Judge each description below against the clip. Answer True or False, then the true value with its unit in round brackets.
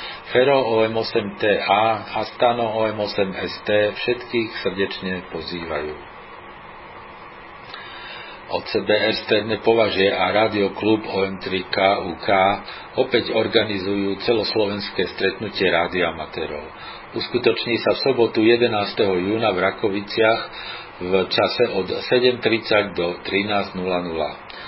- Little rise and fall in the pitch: False (3.1 semitones)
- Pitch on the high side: False (100 Hz)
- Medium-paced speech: False (80 wpm)